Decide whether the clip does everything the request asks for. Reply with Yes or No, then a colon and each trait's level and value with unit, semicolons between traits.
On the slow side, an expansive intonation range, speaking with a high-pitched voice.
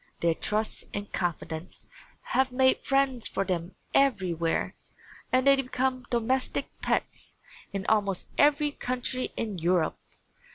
Yes: slow, 120 wpm; wide, 6.3 semitones; high, 225 Hz